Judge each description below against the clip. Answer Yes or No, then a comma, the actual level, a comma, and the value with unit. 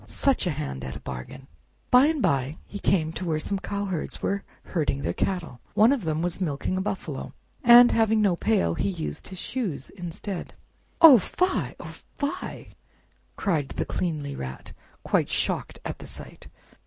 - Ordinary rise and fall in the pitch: No, wide, 5.9 semitones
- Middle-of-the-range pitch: Yes, medium, 180 Hz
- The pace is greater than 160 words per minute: Yes, average, 170 wpm